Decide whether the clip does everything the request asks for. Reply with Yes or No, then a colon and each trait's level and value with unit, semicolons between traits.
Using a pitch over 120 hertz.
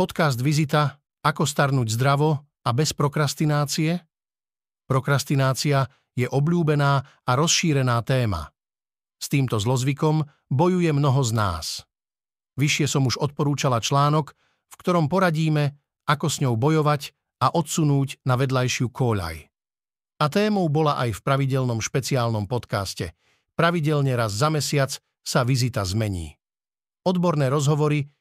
Yes: medium, 140 Hz